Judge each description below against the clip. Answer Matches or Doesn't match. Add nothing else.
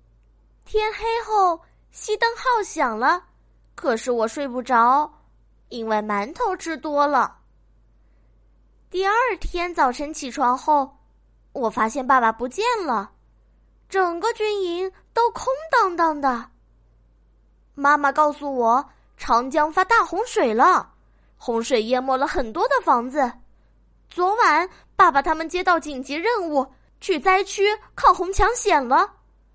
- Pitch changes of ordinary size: Doesn't match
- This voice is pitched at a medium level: Doesn't match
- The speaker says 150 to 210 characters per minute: Matches